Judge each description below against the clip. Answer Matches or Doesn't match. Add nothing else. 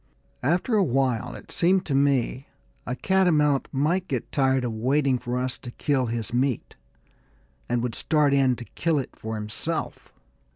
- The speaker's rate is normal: Matches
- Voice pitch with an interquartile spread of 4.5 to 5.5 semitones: Doesn't match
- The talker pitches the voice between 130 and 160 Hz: Matches